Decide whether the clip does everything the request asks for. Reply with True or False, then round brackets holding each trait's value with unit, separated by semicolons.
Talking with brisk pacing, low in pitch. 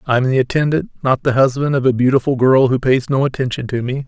True (250 wpm; 130 Hz)